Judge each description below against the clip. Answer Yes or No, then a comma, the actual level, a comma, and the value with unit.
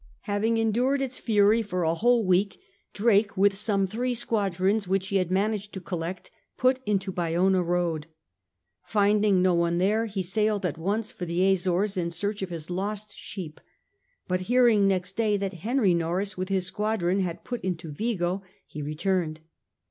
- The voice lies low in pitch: No, high, 195 Hz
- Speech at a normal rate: Yes, average, 170 wpm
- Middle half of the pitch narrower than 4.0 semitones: Yes, average, 3.1 semitones